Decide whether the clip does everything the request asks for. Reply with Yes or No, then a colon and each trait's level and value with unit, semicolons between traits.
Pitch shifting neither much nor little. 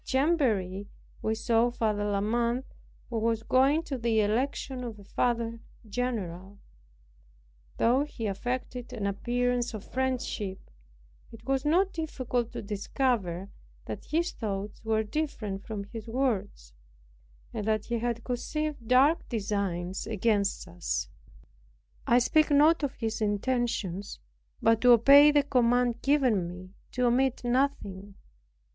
Yes: average, 4.0 semitones